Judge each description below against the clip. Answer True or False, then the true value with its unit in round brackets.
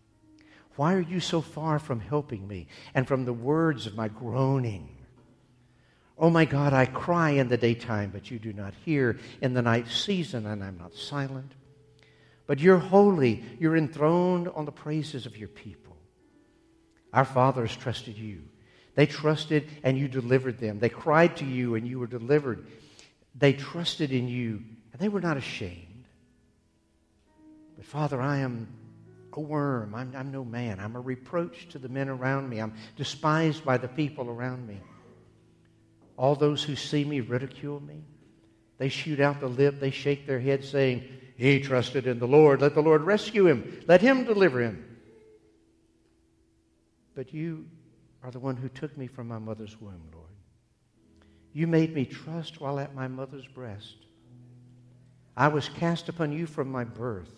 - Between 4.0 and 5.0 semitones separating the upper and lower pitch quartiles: True (4.4 semitones)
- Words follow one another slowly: False (165 wpm)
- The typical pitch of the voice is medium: False (130 Hz)